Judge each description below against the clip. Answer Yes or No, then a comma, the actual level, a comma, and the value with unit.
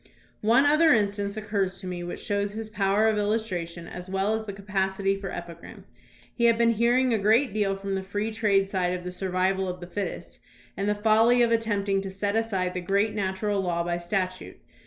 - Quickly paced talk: Yes, fast, 210 wpm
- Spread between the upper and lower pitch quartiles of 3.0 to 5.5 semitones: No, narrow, 2.4 semitones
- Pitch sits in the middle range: No, high, 200 Hz